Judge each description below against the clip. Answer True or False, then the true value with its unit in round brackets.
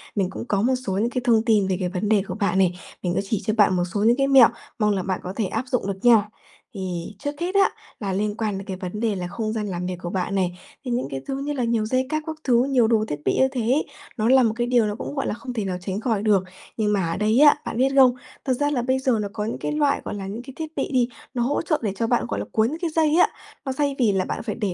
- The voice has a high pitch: True (220 Hz)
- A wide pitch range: False (4.7 semitones)